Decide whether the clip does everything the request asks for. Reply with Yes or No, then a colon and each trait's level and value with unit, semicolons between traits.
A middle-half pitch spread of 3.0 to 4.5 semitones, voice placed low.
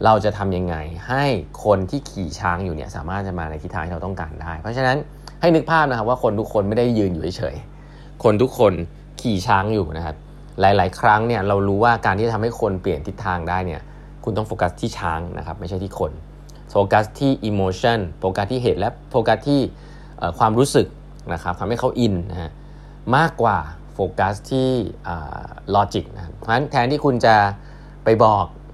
No: average, 5.1 semitones; low, 105 Hz